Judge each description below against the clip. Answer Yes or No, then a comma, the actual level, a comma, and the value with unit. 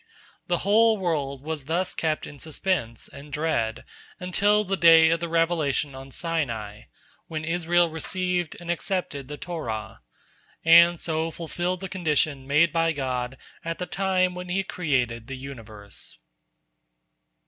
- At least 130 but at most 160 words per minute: Yes, average, 140 wpm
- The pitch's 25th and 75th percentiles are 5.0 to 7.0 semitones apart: No, average, 4.3 semitones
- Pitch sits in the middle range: Yes, medium, 160 Hz